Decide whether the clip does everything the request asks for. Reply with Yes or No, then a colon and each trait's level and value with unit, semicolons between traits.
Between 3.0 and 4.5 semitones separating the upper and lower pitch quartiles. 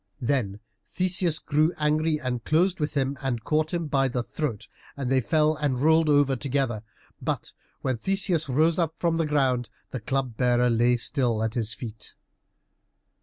Yes: average, 4.2 semitones